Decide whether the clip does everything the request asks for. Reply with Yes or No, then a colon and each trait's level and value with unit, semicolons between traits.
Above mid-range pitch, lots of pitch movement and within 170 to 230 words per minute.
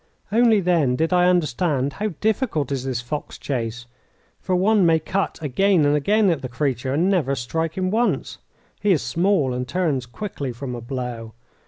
No: medium, 155 Hz; wide, 6.5 semitones; average, 180 wpm